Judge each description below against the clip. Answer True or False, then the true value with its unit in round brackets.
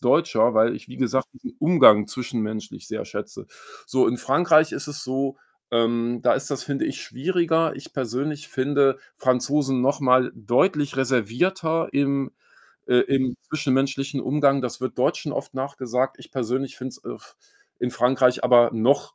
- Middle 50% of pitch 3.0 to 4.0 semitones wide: False (2.5 semitones)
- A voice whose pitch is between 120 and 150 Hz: True (130 Hz)